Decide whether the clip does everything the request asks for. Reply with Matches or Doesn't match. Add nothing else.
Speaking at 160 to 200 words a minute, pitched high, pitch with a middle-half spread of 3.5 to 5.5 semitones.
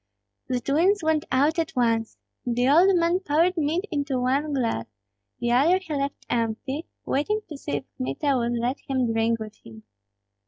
Matches